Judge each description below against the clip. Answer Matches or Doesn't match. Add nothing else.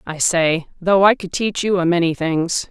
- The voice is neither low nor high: Matches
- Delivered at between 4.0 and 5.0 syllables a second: Matches